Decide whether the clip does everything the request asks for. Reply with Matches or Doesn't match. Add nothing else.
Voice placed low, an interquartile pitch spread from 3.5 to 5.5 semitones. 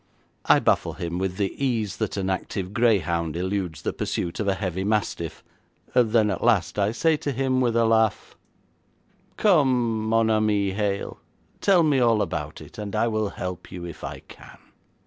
Matches